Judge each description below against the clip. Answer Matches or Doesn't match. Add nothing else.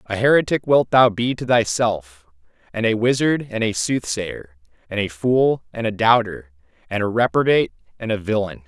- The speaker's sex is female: Doesn't match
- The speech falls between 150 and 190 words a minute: Matches